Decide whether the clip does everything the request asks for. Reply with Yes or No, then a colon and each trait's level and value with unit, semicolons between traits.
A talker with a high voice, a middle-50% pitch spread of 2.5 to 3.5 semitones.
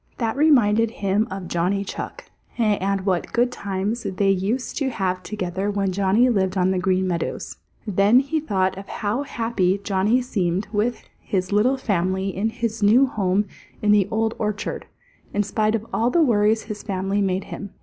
Yes: high, 205 Hz; average, 3.1 semitones